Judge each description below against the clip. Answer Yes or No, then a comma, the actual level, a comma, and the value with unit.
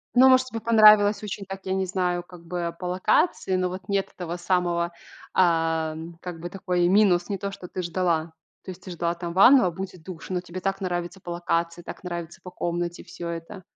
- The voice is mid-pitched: Yes, medium, 180 Hz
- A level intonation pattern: Yes, narrow, 1.9 semitones